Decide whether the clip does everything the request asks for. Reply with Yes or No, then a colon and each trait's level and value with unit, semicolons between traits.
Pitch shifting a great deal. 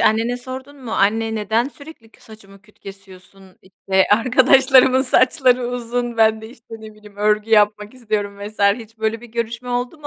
No: average, 2.8 semitones